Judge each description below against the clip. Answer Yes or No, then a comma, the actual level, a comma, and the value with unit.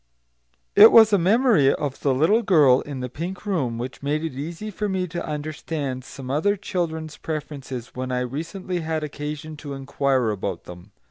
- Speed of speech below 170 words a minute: No, average, 180 wpm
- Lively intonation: No, average, 4.9 semitones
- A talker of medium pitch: Yes, medium, 150 Hz